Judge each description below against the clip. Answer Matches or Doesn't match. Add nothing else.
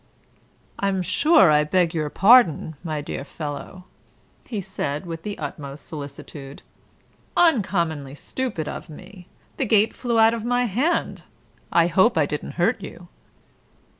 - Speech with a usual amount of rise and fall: Doesn't match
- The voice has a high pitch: Doesn't match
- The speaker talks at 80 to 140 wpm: Matches